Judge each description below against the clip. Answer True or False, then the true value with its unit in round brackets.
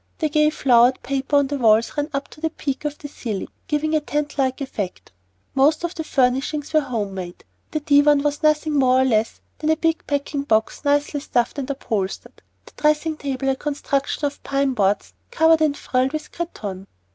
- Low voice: False (285 Hz)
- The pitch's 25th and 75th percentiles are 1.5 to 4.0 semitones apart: True (3.0 semitones)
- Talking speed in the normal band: True (195 wpm)